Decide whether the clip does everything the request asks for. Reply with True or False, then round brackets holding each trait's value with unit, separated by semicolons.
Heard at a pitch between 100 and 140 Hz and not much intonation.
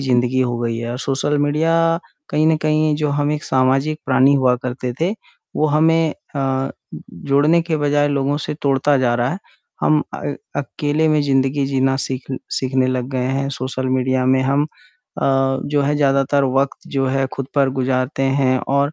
True (135 Hz; 2.0 semitones)